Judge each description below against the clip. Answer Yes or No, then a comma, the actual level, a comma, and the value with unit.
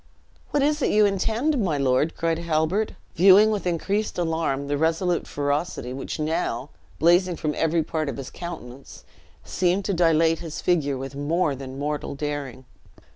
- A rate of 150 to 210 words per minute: Yes, average, 160 wpm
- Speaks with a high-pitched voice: No, medium, 160 Hz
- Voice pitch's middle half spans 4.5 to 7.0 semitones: No, average, 4.0 semitones